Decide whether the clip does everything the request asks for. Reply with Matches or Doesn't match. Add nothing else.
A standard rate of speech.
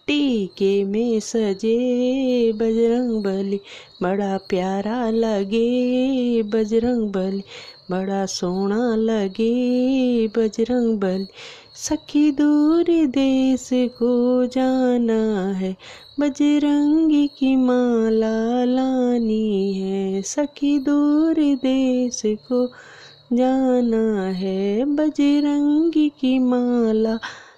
Doesn't match